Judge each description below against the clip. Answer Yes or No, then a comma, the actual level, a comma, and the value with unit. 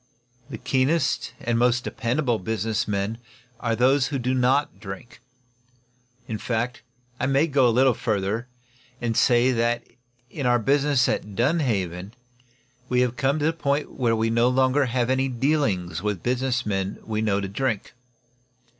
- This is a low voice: Yes, low, 120 Hz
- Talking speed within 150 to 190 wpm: Yes, average, 160 wpm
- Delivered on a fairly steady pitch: No, average, 3.1 semitones